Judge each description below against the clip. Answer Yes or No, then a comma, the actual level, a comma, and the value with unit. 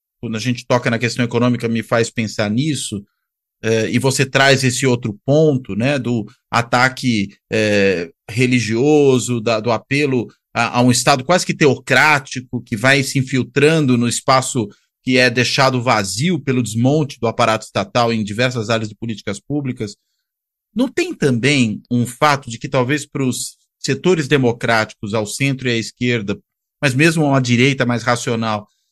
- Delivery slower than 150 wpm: No, average, 160 wpm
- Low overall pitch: Yes, low, 125 Hz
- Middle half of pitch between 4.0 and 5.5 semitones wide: No, average, 3.0 semitones